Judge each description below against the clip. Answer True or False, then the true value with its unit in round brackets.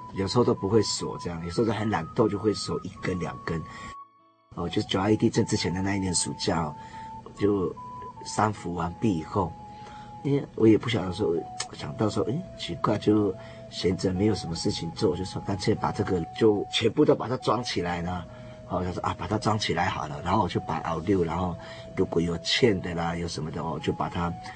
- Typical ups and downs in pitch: True (3.9 semitones)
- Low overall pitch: True (105 Hz)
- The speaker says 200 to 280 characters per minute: False (300 characters per minute)